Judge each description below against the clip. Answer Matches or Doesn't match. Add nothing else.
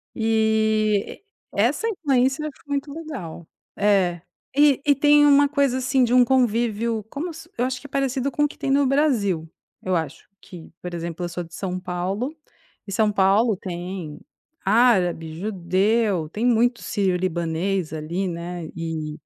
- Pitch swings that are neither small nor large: Doesn't match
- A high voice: Matches